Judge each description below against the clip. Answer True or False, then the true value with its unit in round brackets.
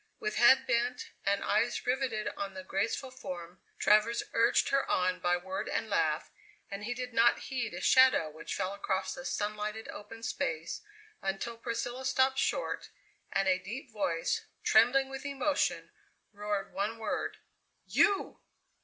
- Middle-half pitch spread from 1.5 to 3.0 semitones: False (4.7 semitones)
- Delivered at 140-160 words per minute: True (150 wpm)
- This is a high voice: True (225 Hz)